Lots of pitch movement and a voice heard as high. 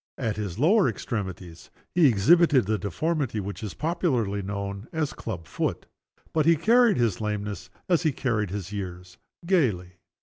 No: wide, 8.0 semitones; low, 110 Hz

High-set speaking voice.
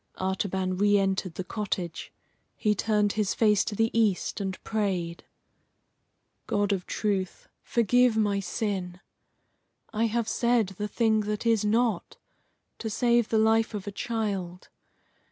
Yes: high, 210 Hz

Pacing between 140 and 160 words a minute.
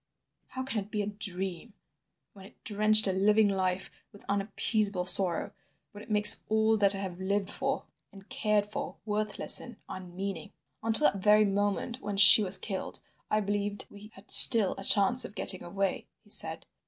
No: average, 180 wpm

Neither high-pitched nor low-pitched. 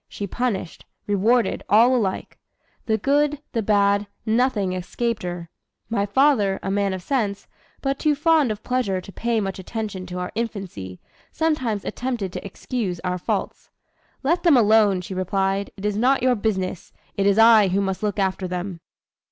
No: high, 205 Hz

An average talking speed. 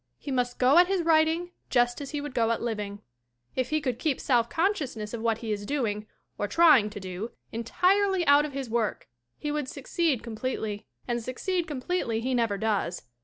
Yes: average, 195 wpm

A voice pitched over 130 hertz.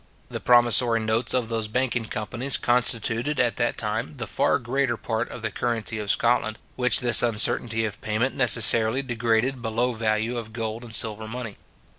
No: low, 115 Hz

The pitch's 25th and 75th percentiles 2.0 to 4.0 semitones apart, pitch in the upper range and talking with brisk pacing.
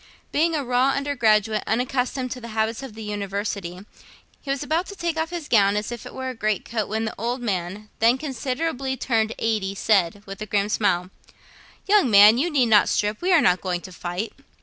No: average, 4.5 semitones; high, 225 Hz; fast, 210 wpm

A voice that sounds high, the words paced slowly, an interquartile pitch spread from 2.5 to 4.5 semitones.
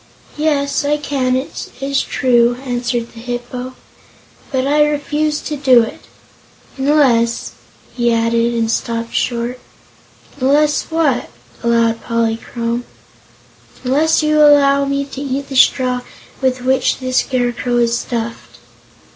Yes: very high, 255 Hz; slow, 130 wpm; average, 2.9 semitones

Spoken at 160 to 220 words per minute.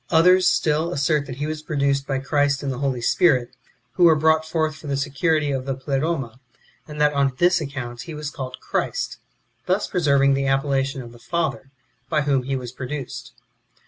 Yes: average, 195 wpm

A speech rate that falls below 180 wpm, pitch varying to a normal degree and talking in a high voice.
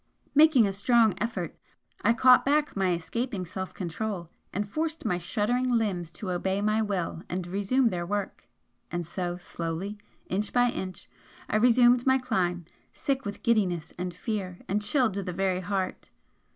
Yes: average, 165 wpm; average, 4.7 semitones; high, 200 Hz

